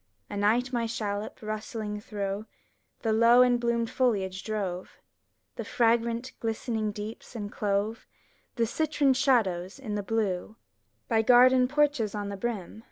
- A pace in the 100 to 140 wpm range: Yes, slow, 135 wpm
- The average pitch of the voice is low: No, high, 225 Hz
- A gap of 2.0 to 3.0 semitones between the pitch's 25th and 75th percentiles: Yes, average, 2.7 semitones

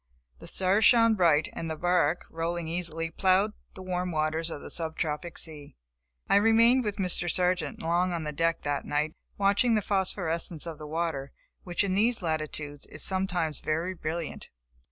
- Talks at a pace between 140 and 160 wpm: No, average, 170 wpm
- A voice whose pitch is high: No, medium, 170 Hz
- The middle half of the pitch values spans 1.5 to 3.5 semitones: Yes, average, 3.1 semitones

